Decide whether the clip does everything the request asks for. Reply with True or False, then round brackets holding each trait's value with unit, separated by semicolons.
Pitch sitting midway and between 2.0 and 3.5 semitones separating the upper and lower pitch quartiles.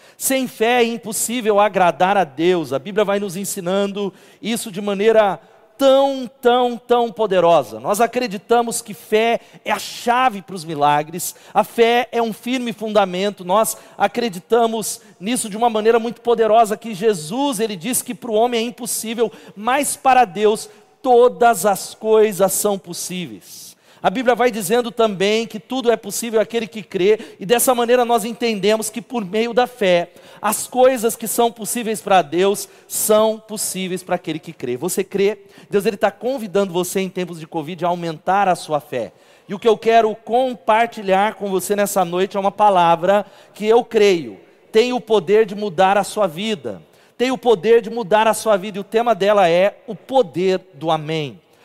False (215 Hz; 3.2 semitones)